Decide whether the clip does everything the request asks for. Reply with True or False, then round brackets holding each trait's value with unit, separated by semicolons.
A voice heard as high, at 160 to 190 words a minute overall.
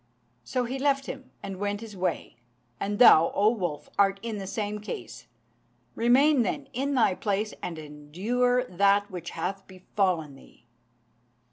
False (205 Hz; 150 wpm)